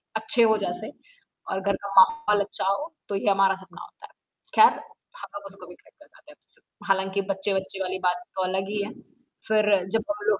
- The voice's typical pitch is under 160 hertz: No, high, 200 Hz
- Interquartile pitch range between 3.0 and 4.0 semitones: No, narrow, 2.4 semitones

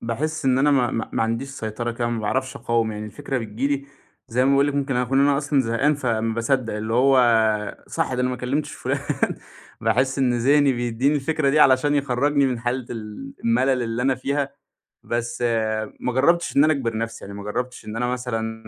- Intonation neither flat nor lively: Yes, average, 3.1 semitones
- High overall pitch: No, low, 125 Hz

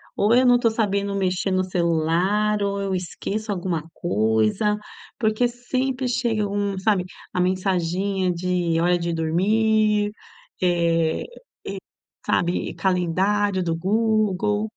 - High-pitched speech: Yes, high, 195 Hz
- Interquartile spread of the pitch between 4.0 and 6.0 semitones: No, average, 3.3 semitones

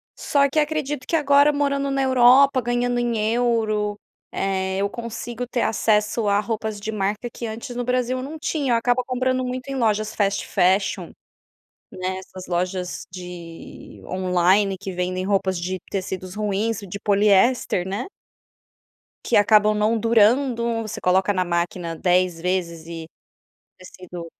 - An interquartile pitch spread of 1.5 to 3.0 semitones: No, average, 4.7 semitones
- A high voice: Yes, high, 210 Hz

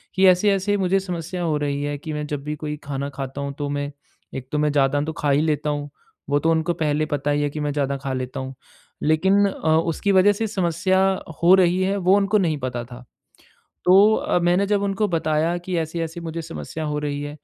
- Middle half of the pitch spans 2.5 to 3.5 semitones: No, average, 4.1 semitones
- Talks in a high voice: No, medium, 155 Hz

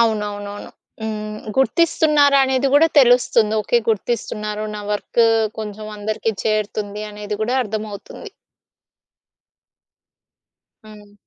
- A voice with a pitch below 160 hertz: No, high, 215 Hz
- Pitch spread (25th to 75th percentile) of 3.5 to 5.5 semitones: No, average, 2.7 semitones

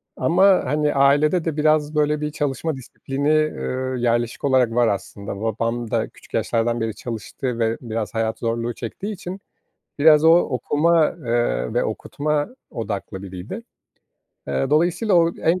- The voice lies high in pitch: No, low, 135 Hz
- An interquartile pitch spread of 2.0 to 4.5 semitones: No, average, 5.0 semitones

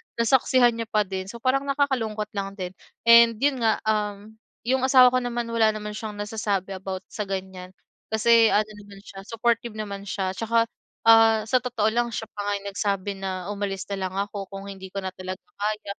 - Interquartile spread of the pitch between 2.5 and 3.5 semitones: Yes, average, 2.8 semitones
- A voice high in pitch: Yes, high, 210 Hz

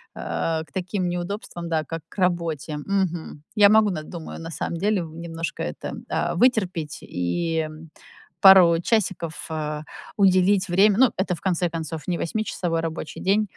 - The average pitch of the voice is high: No, medium, 175 Hz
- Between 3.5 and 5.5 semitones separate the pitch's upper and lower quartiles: No, average, 2.9 semitones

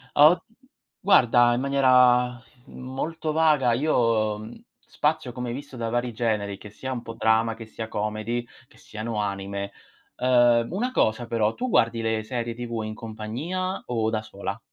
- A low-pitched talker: Yes, low, 120 Hz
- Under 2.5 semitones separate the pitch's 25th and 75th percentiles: No, average, 2.8 semitones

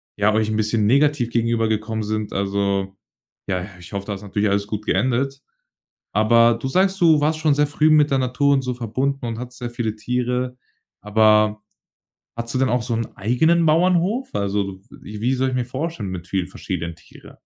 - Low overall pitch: Yes, low, 115 Hz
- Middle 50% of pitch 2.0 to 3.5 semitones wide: No, average, 4.2 semitones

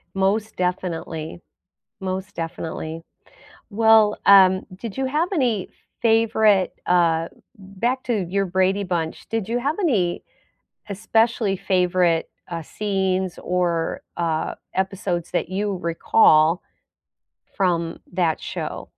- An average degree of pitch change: Yes, average, 3.6 semitones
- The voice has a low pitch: No, high, 190 Hz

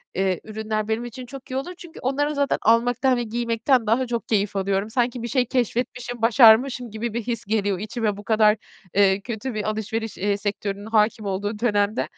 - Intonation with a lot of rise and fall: No, average, 2.7 semitones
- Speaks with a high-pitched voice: Yes, high, 225 Hz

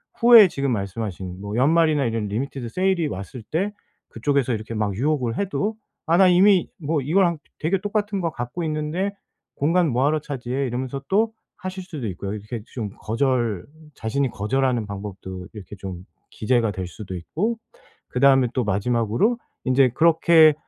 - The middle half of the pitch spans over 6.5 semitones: Yes, wide, 7.3 semitones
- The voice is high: No, low, 130 Hz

